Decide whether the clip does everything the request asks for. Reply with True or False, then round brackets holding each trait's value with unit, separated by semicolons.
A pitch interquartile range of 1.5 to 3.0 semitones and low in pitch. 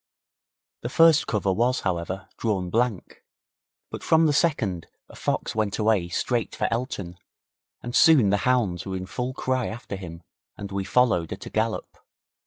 False (4.9 semitones; 110 Hz)